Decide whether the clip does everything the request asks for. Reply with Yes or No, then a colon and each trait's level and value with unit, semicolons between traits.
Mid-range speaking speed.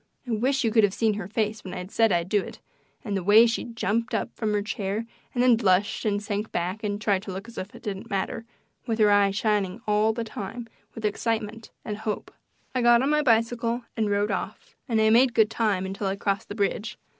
No: fast, 235 wpm